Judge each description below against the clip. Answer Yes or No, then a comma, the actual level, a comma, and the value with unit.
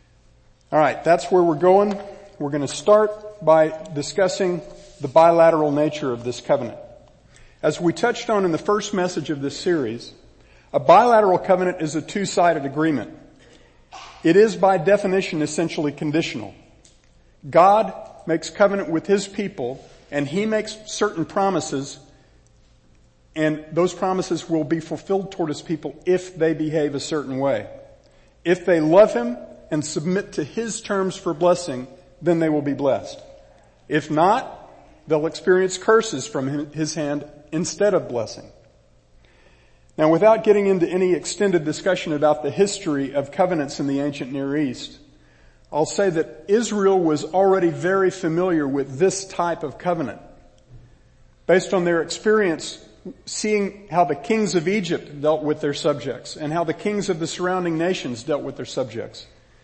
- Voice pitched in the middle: Yes, medium, 165 Hz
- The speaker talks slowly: No, average, 150 wpm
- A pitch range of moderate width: Yes, average, 4.3 semitones